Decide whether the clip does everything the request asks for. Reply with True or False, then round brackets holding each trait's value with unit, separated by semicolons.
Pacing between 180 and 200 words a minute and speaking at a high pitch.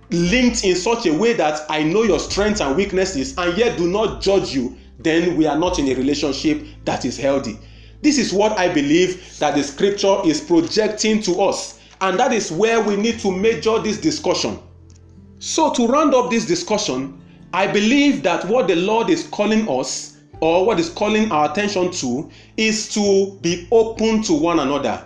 True (190 wpm; 195 Hz)